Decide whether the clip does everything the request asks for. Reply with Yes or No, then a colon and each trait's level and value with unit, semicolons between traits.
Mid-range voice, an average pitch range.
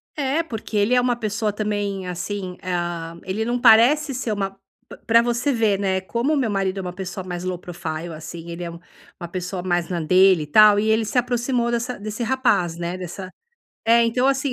No: high, 205 Hz; average, 4.7 semitones